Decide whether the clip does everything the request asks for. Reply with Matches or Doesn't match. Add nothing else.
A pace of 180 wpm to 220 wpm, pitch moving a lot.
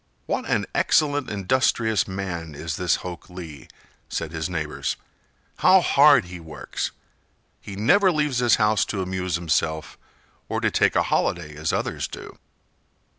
Doesn't match